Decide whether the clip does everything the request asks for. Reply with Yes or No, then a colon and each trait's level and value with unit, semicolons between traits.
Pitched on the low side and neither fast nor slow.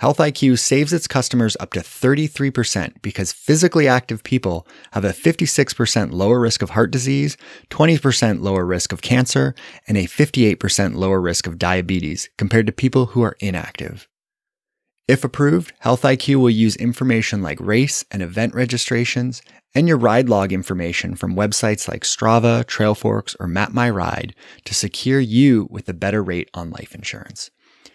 Yes: low, 115 Hz; average, 155 wpm